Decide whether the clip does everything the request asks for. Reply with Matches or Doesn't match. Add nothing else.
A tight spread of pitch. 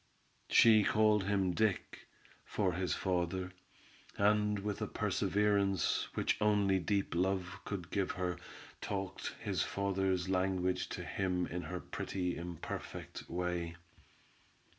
Matches